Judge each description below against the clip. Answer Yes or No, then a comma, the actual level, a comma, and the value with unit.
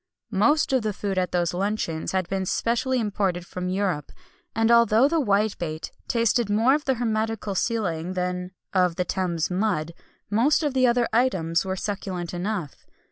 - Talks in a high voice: Yes, high, 200 Hz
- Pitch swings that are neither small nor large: Yes, average, 4.4 semitones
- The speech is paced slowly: No, average, 165 wpm